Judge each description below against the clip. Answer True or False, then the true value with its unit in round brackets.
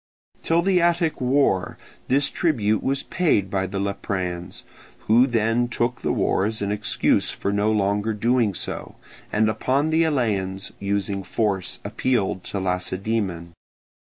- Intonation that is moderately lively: True (4.5 semitones)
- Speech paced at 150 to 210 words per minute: False (140 wpm)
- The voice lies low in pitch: True (105 Hz)